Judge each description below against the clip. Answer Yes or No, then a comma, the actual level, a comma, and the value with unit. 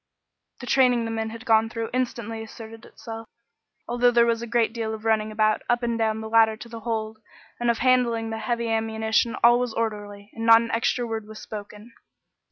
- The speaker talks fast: Yes, fast, 210 wpm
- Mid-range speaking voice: No, high, 225 Hz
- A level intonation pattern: Yes, narrow, 1.2 semitones